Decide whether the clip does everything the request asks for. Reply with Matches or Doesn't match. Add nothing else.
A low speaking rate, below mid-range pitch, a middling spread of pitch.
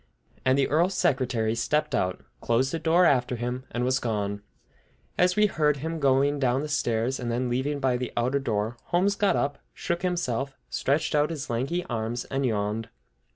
Doesn't match